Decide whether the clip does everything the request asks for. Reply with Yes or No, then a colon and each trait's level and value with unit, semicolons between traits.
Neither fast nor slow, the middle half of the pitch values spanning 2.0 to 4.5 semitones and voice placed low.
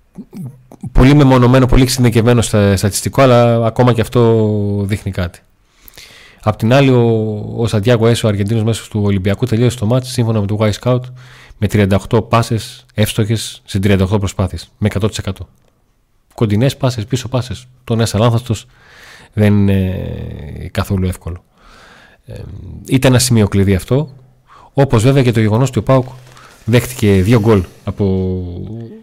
Yes: average, 145 wpm; average, 3.5 semitones; low, 115 Hz